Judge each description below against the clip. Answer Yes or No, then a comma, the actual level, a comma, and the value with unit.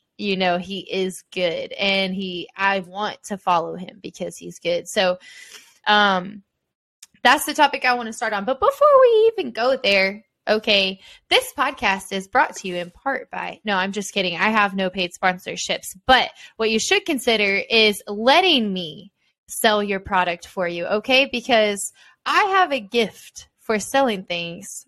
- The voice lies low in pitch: No, high, 210 Hz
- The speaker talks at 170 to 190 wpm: Yes, average, 175 wpm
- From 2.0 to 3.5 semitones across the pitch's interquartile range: No, average, 5.0 semitones